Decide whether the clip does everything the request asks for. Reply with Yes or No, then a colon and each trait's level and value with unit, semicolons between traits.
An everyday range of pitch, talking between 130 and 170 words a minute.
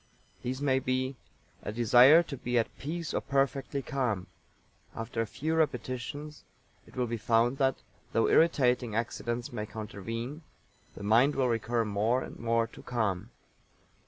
Yes: average, 3.1 semitones; average, 150 wpm